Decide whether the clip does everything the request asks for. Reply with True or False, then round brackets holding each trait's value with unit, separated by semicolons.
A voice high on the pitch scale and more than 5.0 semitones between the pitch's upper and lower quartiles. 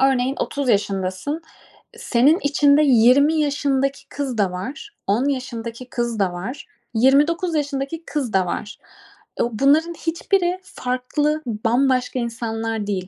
False (265 Hz; 4.5 semitones)